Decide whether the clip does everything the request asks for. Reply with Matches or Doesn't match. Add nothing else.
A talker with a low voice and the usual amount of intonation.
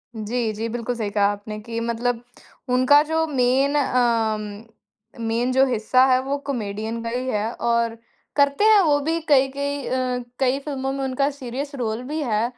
Doesn't match